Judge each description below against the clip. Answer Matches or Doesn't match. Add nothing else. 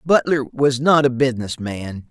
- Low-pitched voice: Matches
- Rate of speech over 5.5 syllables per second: Doesn't match